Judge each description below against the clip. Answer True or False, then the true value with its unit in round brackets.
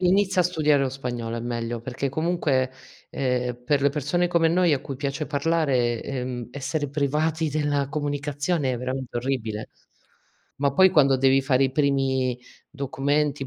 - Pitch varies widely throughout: False (2.8 semitones)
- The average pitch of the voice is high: False (140 Hz)